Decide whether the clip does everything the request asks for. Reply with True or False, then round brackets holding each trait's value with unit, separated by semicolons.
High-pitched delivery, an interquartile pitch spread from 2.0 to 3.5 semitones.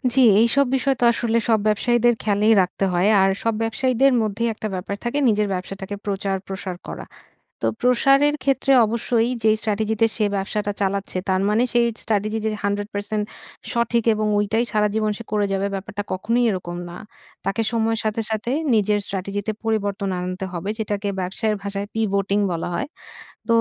True (210 Hz; 2.4 semitones)